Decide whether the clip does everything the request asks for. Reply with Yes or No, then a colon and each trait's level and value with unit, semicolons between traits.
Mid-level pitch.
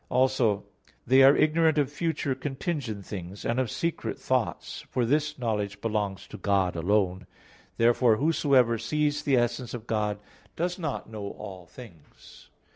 No: low, 120 Hz